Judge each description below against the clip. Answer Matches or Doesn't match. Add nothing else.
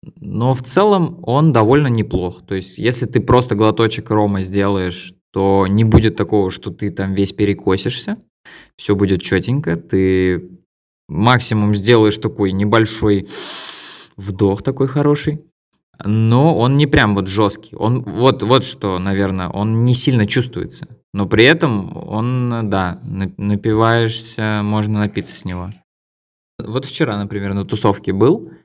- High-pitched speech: Doesn't match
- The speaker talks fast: Doesn't match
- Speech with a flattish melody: Doesn't match